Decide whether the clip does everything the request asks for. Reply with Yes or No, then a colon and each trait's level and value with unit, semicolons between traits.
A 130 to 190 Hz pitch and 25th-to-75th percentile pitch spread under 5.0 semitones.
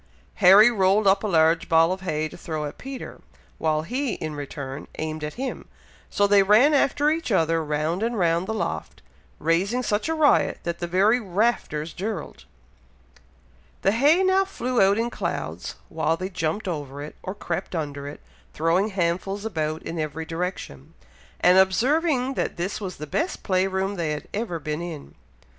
No: medium, 185 Hz; wide, 5.4 semitones